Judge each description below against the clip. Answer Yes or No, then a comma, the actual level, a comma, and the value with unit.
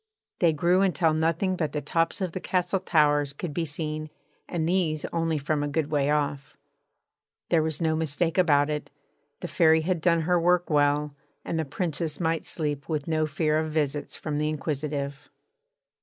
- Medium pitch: Yes, medium, 155 Hz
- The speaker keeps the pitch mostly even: Yes, narrow, 2.2 semitones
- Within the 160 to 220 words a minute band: Yes, average, 180 wpm